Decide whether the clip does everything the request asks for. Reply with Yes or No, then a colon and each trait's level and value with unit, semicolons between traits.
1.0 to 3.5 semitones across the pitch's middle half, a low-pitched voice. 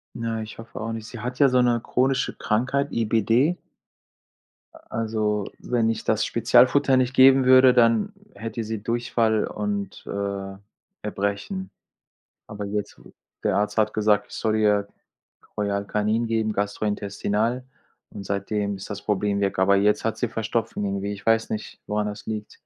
Yes: narrow, 2.6 semitones; low, 110 Hz